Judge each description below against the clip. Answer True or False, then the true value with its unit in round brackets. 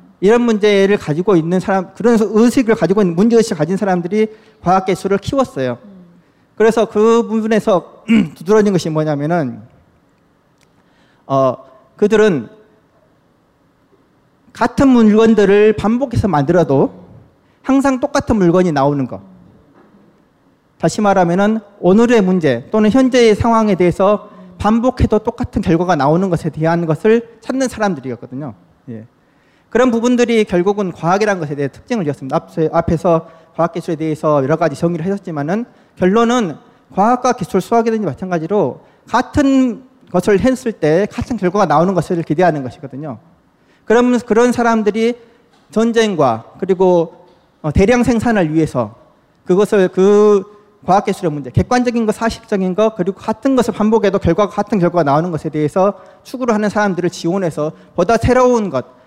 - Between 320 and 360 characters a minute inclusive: True (325 characters per minute)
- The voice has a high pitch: True (195 Hz)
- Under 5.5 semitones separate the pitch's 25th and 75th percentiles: True (5.1 semitones)